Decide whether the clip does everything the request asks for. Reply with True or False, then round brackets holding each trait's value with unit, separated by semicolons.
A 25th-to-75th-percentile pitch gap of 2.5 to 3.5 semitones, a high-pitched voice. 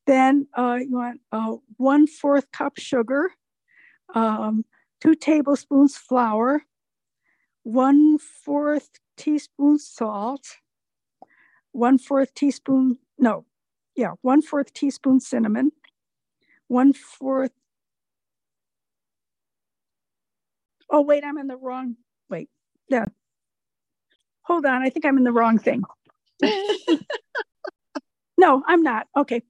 True (3.1 semitones; 270 Hz)